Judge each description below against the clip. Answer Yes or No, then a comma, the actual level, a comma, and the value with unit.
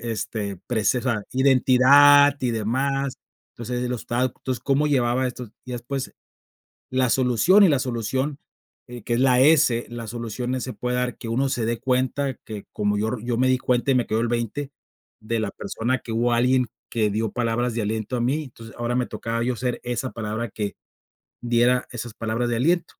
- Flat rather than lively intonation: Yes, narrow, 2.1 semitones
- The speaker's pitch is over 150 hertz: No, low, 120 Hz